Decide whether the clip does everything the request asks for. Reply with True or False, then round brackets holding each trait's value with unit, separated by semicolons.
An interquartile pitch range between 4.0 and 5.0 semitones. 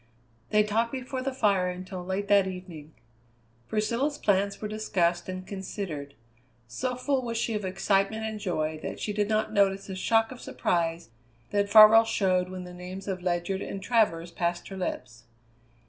False (3.3 semitones)